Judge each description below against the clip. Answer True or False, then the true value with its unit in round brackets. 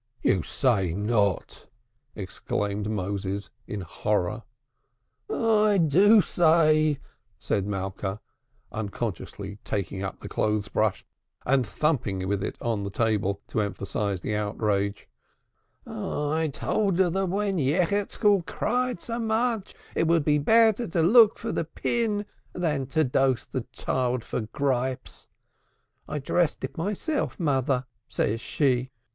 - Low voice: True (130 Hz)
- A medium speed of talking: False (125 wpm)